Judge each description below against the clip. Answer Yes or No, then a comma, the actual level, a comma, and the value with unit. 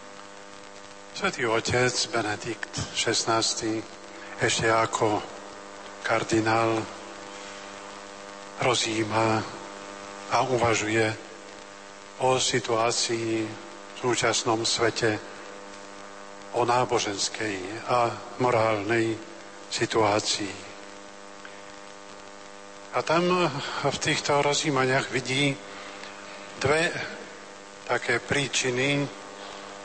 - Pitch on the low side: Yes, low, 100 Hz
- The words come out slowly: Yes, slow, 60 wpm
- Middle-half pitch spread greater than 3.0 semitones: No, narrow, 2.6 semitones